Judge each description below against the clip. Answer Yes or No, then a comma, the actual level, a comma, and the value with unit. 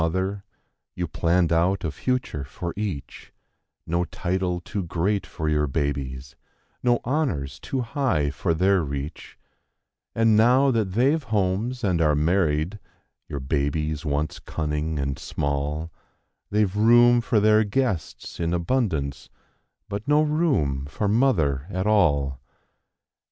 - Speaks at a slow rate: Yes, slow, 130 wpm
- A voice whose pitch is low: Yes, very low, 90 Hz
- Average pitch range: No, wide, 6.4 semitones